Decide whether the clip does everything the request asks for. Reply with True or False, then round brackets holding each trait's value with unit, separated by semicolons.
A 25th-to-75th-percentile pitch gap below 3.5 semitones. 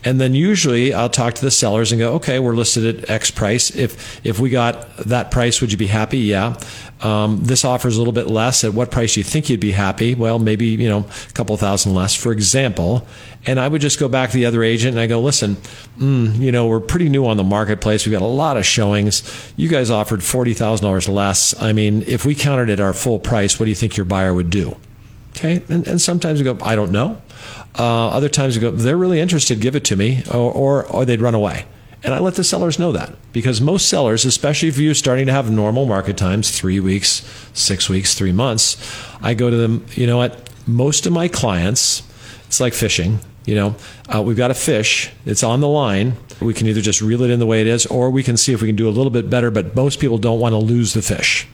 True (3.1 semitones)